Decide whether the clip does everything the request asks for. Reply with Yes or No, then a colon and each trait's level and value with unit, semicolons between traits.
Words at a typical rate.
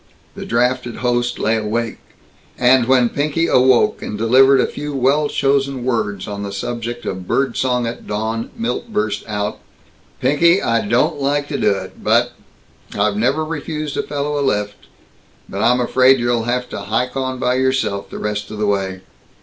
Yes: average, 175 wpm